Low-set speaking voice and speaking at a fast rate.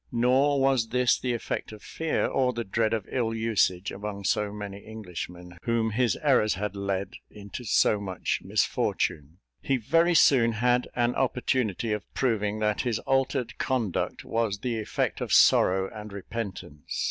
No: low, 110 Hz; average, 160 wpm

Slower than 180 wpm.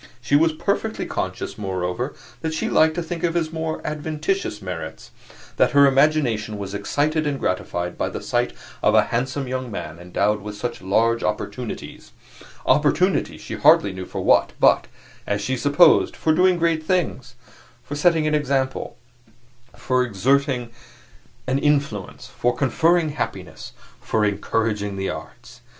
Yes: average, 150 wpm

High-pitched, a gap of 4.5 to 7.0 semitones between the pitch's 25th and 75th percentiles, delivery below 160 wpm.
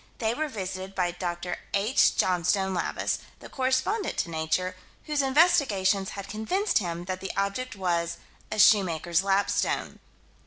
Yes: high, 195 Hz; average, 5.2 semitones; average, 140 wpm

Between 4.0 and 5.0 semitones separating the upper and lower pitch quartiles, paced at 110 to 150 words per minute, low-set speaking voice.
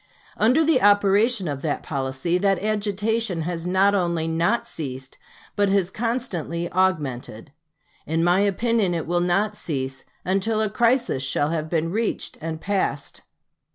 No: average, 4.6 semitones; average, 145 wpm; medium, 185 Hz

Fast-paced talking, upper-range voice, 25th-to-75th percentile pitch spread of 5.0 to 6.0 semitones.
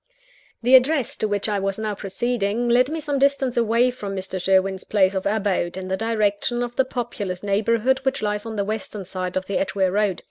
No: fast, 210 wpm; high, 210 Hz; average, 3.8 semitones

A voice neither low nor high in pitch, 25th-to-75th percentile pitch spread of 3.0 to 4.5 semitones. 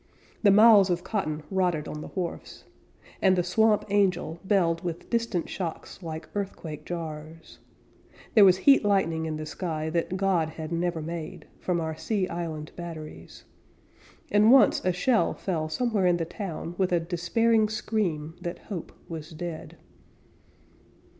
Yes: medium, 175 Hz; average, 3.5 semitones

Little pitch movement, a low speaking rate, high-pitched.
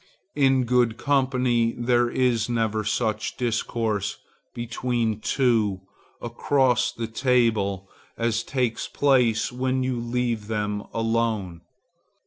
No: narrow, 2.3 semitones; slow, 105 wpm; low, 115 Hz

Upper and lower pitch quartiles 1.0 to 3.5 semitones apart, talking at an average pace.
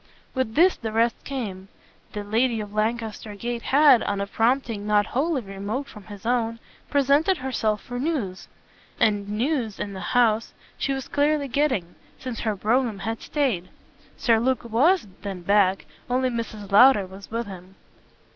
No: average, 4.1 semitones; average, 160 wpm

